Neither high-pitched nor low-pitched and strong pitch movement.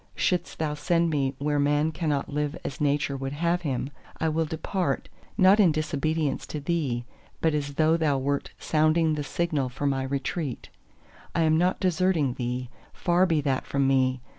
No: medium, 150 Hz; average, 2.9 semitones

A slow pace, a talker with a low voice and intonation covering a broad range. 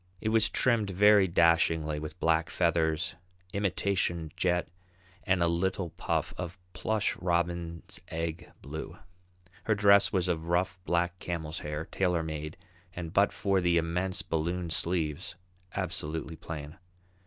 No: slow, 130 wpm; very low, 85 Hz; narrow, 2.5 semitones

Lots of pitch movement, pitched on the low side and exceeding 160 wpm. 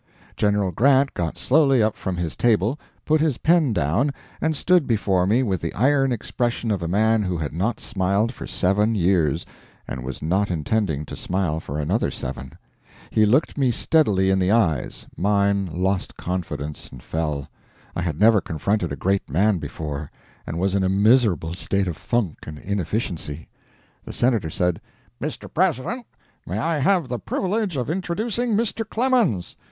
Yes: wide, 6.6 semitones; low, 100 Hz; average, 170 wpm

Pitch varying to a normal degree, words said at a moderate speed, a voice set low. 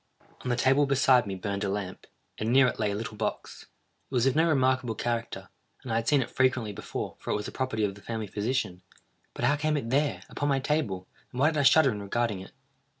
No: average, 4.3 semitones; fast, 250 wpm; low, 120 Hz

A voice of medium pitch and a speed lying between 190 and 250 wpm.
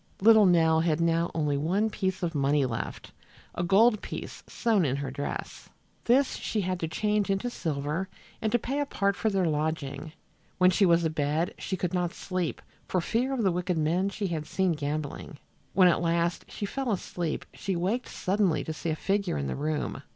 Yes: medium, 175 Hz; average, 195 wpm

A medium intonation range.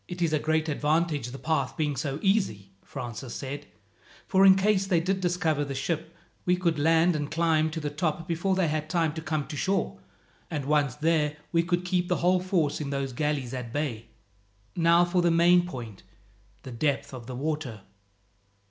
Yes: average, 3.5 semitones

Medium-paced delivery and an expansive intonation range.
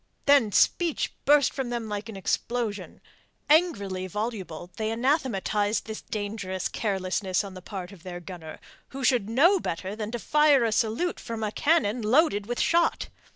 No: average, 160 wpm; average, 4.7 semitones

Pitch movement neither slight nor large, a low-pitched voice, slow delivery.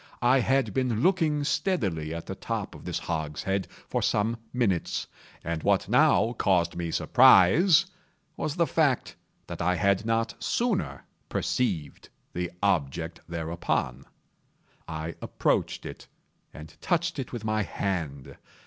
No: wide, 7.6 semitones; low, 100 Hz; slow, 130 wpm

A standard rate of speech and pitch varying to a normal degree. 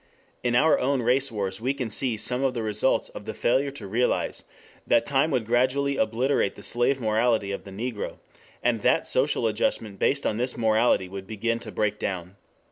Yes: average, 195 wpm; average, 3.4 semitones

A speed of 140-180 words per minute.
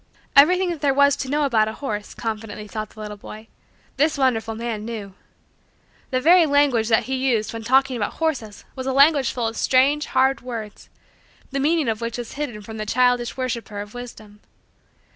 No: average, 190 wpm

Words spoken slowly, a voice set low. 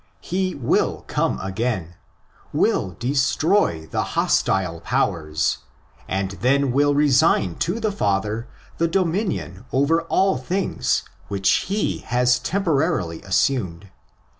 Yes: slow, 110 wpm; low, 125 Hz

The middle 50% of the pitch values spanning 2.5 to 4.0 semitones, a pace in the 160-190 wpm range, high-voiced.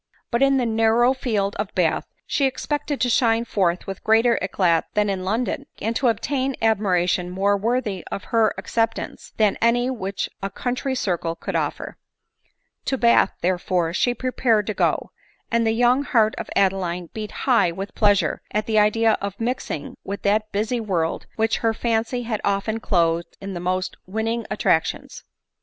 Yes: average, 3.5 semitones; average, 170 wpm; high, 220 Hz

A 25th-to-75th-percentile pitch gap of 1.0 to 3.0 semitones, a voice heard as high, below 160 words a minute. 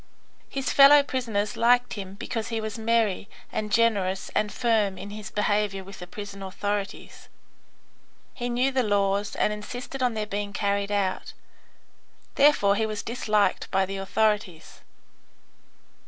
Yes: narrow, 2.5 semitones; high, 210 Hz; average, 140 wpm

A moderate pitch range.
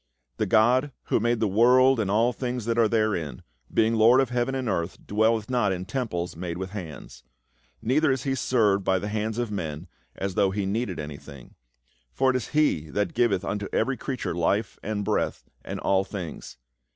Yes: average, 4.5 semitones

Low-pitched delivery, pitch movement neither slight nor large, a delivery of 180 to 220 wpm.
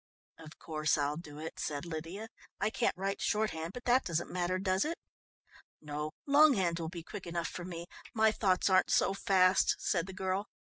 No: medium, 185 Hz; average, 3.3 semitones; average, 185 wpm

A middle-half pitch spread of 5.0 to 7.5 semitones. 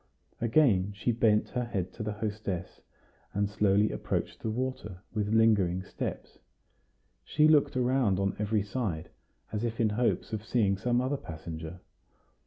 No: average, 3.5 semitones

